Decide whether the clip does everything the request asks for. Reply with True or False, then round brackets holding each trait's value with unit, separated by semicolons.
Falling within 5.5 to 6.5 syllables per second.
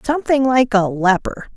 False (5.3 syllables/s)